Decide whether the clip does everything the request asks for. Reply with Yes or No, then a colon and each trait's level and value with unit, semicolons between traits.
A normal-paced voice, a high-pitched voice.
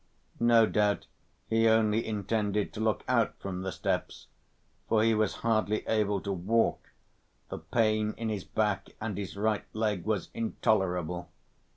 No: average, 150 wpm; low, 110 Hz